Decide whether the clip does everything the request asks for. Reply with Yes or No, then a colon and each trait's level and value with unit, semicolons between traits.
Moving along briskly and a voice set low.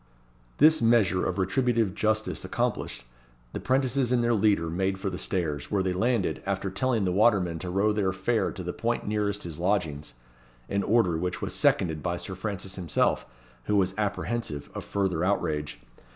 No: average, 175 wpm; very low, 95 Hz